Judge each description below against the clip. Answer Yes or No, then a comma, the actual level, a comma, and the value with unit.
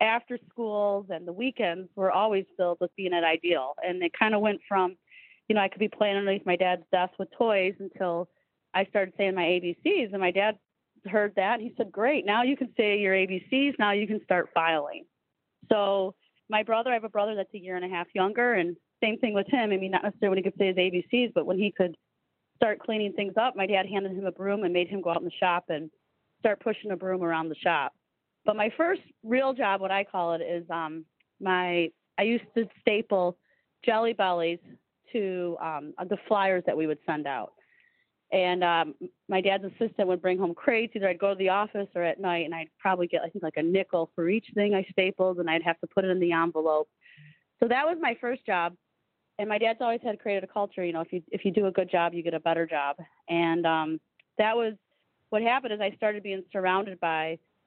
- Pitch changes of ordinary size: Yes, average, 3.4 semitones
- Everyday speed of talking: No, fast, 235 wpm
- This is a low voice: No, high, 195 Hz